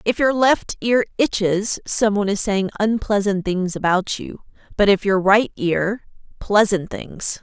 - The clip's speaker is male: No, female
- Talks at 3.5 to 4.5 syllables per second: Yes, 4.1 syllables/s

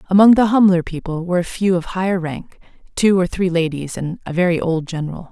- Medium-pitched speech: Yes, medium, 175 Hz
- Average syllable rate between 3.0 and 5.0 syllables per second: No, 5.9 syllables/s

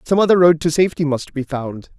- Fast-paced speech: Yes, fast, 240 wpm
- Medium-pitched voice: Yes, medium, 155 Hz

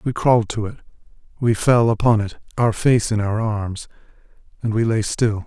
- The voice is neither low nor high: No, low, 110 Hz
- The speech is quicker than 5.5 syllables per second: No, 5.0 syllables/s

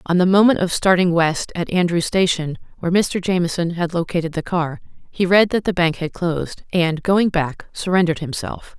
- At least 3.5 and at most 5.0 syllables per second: No, 5.3 syllables/s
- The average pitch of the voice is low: No, medium, 175 Hz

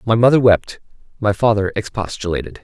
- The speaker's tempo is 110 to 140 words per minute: Yes, slow, 135 wpm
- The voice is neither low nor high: No, low, 105 Hz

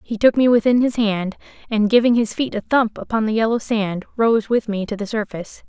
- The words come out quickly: Yes, fast, 230 wpm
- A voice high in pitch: Yes, high, 220 Hz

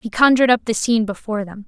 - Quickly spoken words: Yes, fast, 250 wpm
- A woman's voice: Yes, female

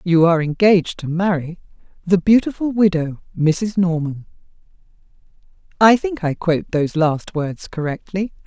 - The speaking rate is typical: No, slow, 130 wpm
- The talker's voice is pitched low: No, medium, 175 Hz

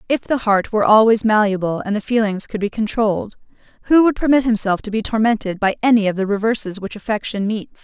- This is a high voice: Yes, high, 215 Hz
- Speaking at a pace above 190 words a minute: Yes, fast, 205 wpm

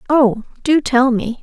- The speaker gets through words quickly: No, average, 170 wpm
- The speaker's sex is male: No, female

